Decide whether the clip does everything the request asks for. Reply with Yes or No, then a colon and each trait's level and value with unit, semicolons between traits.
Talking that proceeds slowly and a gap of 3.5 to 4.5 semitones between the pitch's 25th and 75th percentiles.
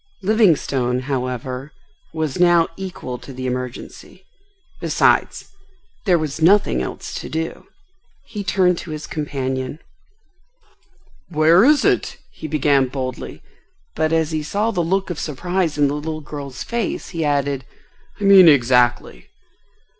No: slow, 130 wpm; average, 5.0 semitones